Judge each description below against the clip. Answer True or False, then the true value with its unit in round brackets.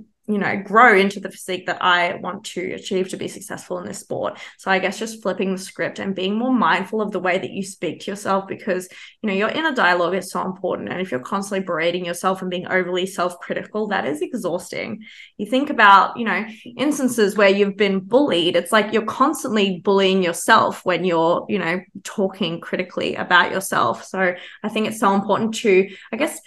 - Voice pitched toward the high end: True (195 Hz)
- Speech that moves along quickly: True (210 wpm)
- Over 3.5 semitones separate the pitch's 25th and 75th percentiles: False (2.8 semitones)